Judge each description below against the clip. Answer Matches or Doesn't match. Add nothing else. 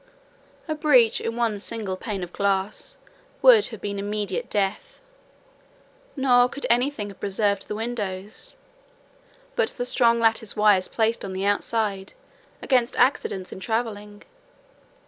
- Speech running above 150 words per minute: Doesn't match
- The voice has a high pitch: Matches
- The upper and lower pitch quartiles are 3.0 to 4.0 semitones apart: Matches